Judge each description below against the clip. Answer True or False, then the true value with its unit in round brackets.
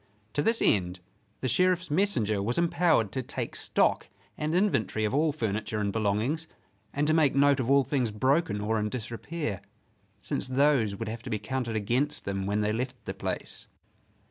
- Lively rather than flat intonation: True (5.7 semitones)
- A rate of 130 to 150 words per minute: False (180 wpm)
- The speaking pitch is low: True (125 Hz)